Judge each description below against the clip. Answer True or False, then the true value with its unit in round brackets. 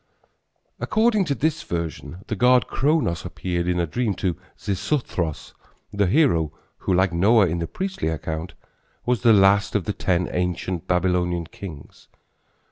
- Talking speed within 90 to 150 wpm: True (145 wpm)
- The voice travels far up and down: True (5.9 semitones)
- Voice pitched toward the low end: True (95 Hz)